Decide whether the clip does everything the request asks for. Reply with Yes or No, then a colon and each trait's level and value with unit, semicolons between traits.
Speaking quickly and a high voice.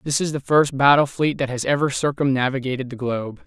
No: fast, 210 wpm; low, 135 Hz